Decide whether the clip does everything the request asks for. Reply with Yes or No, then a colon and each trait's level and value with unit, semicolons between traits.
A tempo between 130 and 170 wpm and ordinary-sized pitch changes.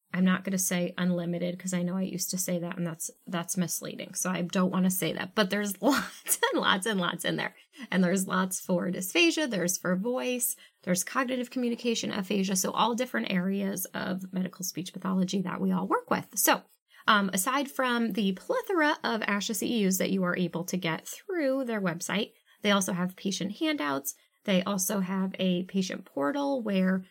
No: average, 195 wpm; average, 4.2 semitones